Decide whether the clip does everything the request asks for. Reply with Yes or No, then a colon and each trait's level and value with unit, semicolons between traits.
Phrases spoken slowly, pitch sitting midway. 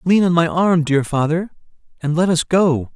No: fast, 205 wpm; medium, 165 Hz